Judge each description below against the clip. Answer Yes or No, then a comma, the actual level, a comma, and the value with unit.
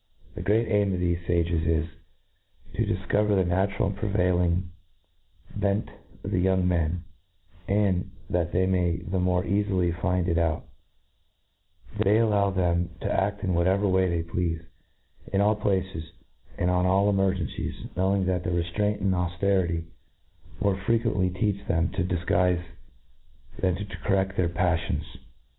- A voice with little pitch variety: Yes, narrow, 2.2 semitones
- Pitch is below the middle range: Yes, very low, 90 Hz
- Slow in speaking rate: No, average, 145 wpm